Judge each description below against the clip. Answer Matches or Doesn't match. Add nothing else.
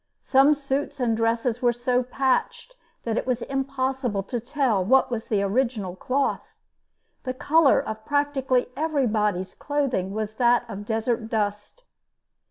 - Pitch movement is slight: Doesn't match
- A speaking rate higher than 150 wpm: Doesn't match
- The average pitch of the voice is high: Matches